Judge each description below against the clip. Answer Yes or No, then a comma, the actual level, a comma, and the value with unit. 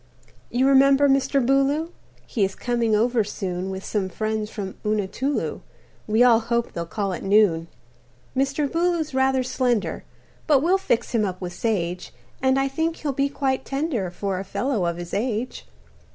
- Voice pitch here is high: Yes, high, 235 Hz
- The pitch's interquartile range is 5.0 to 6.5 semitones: Yes, wide, 5.4 semitones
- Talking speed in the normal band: Yes, average, 165 wpm